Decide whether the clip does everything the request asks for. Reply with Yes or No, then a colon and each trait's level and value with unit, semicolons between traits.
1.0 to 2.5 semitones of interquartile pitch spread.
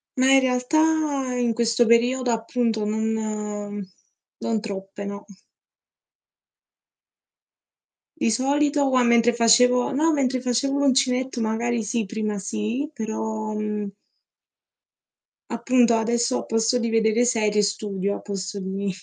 No: average, 2.9 semitones